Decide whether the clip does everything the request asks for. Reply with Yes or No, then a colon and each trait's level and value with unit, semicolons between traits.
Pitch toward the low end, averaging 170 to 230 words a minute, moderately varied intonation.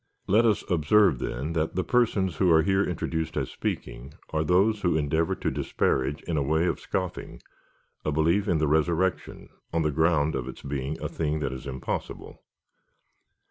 Yes: very low, 80 Hz; average, 180 wpm; average, 3.9 semitones